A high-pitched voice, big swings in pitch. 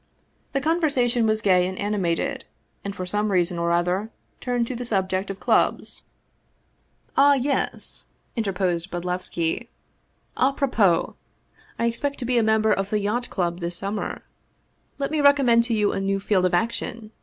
No: high, 210 Hz; average, 4.7 semitones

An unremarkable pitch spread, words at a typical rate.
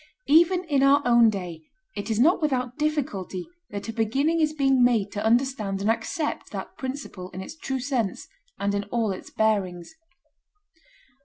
No: wide, 5.7 semitones; average, 165 wpm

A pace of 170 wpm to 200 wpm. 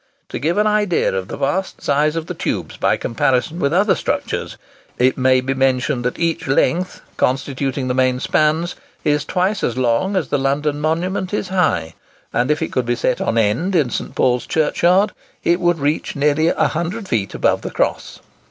Yes: average, 185 wpm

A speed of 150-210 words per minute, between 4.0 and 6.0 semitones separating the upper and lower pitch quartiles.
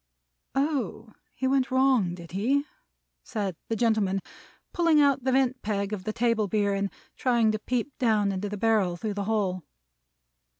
Yes: average, 165 wpm; average, 4.3 semitones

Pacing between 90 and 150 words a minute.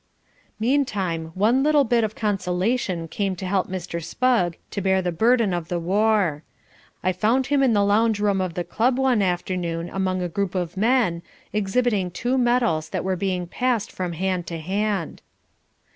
No: average, 175 wpm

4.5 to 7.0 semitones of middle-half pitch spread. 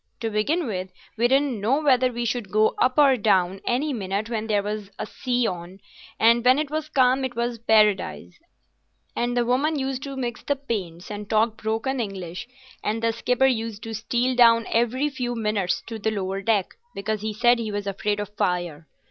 No: average, 3.4 semitones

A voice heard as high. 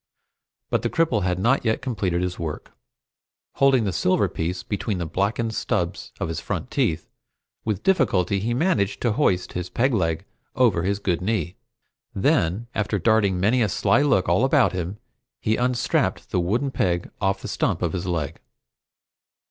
No: low, 100 Hz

